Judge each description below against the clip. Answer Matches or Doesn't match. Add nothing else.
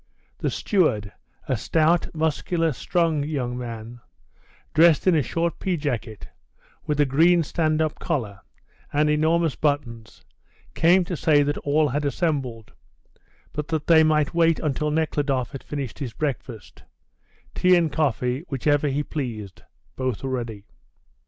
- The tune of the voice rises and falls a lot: Doesn't match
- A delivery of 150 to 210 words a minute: Doesn't match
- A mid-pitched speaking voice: Matches